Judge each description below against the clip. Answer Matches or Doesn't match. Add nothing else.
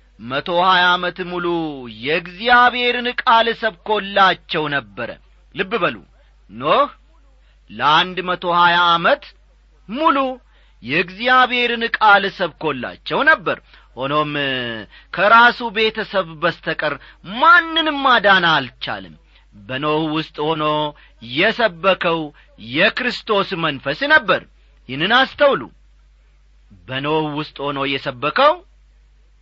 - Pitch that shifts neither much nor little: Doesn't match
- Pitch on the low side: Doesn't match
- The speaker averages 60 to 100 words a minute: Matches